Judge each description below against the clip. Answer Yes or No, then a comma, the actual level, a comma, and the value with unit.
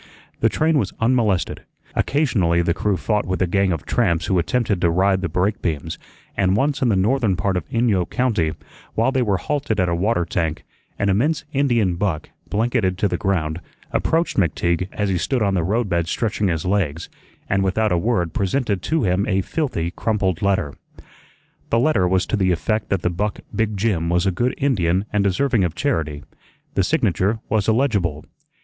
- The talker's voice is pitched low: Yes, very low, 95 Hz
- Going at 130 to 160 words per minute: No, average, 190 wpm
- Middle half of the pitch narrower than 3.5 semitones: No, average, 4.4 semitones